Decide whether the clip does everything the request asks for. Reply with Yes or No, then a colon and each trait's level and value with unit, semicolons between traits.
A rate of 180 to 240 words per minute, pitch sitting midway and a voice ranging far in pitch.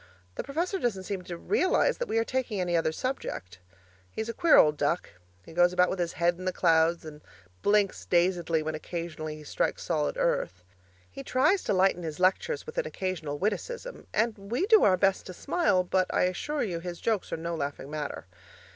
Yes: average, 200 wpm; medium, 180 Hz; wide, 5.7 semitones